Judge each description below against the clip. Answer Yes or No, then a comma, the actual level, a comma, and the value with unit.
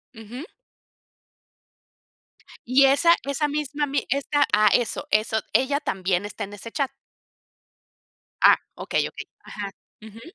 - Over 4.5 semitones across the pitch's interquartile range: Yes, average, 5.1 semitones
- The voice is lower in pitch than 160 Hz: No, very high, 260 Hz